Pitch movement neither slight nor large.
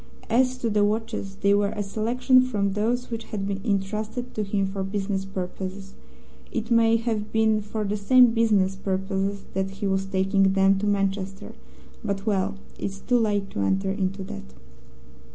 No: narrow, 2.3 semitones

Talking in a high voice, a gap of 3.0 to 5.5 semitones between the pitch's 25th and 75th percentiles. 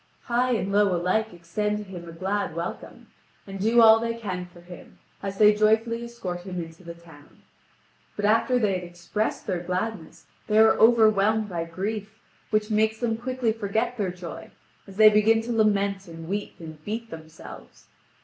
Yes: high, 205 Hz; average, 3.8 semitones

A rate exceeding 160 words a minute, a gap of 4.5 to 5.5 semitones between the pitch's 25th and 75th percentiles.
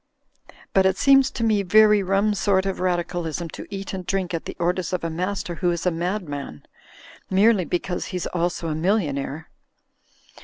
No: average, 175 wpm; narrow, 2.5 semitones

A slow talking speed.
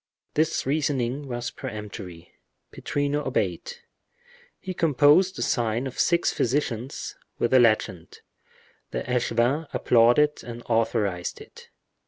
Yes: slow, 105 wpm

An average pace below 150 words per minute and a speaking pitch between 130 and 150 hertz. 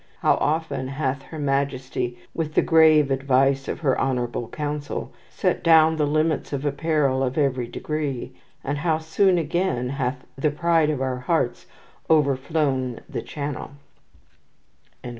Yes: average, 140 wpm; medium, 140 Hz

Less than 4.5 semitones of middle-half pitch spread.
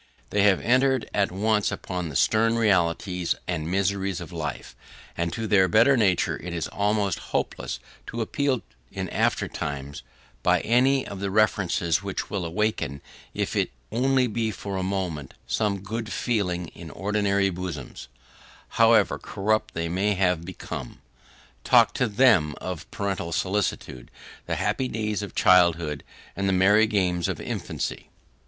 Yes: average, 3.7 semitones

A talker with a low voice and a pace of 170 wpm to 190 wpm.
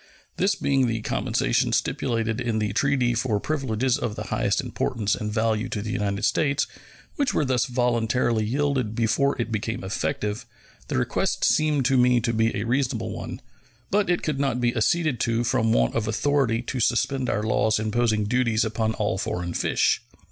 Yes: low, 115 Hz; average, 175 wpm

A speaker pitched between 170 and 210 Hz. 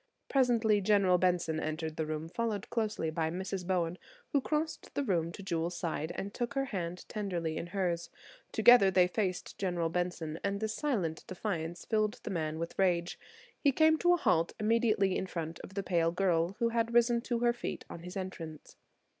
Yes: medium, 185 Hz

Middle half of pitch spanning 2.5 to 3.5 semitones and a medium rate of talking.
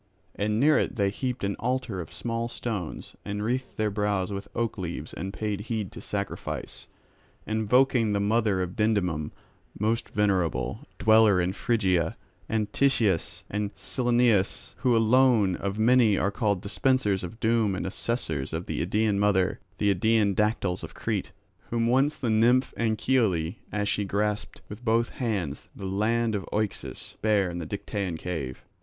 Yes: average, 3.1 semitones; average, 155 wpm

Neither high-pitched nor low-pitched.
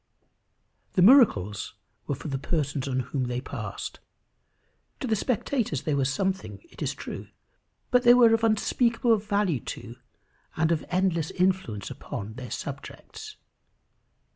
Yes: medium, 175 Hz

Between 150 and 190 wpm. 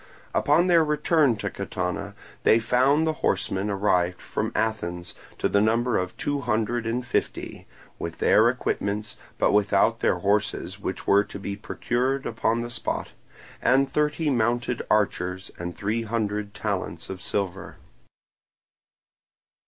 No: slow, 135 wpm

